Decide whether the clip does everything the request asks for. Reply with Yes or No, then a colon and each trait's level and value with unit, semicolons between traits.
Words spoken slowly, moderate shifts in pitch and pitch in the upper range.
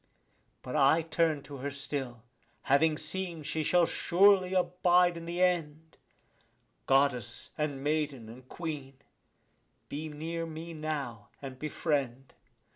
No: slow, 120 wpm; average, 3.5 semitones; medium, 155 Hz